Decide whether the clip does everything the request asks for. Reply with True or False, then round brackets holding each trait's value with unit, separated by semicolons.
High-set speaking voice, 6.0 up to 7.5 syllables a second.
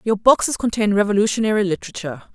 True (210 Hz; 7.2 syllables/s)